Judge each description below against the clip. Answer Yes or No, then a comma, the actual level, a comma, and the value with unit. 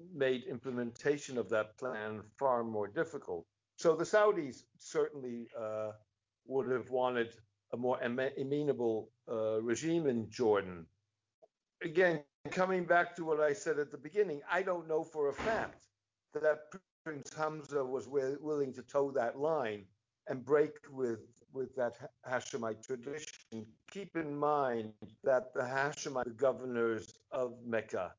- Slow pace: Yes, slow, 140 wpm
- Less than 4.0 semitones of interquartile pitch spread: No, average, 5.1 semitones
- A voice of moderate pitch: No, low, 130 Hz